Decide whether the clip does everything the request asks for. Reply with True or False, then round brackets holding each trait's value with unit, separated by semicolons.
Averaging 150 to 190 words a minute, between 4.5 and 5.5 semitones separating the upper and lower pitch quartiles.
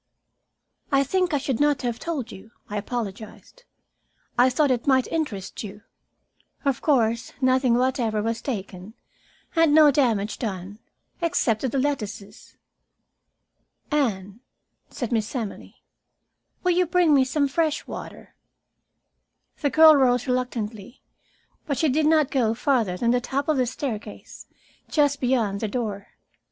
False (140 wpm; 4.8 semitones)